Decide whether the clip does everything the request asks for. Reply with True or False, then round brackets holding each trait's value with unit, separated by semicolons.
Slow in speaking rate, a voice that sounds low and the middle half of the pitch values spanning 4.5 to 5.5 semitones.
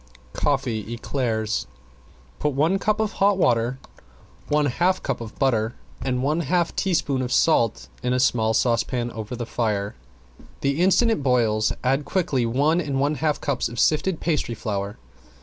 False (160 wpm; 130 Hz; 4.9 semitones)